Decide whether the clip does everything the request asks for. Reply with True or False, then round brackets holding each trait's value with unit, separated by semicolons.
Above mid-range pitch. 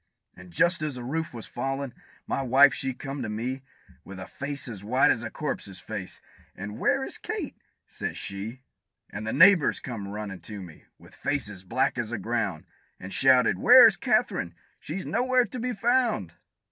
False (120 Hz)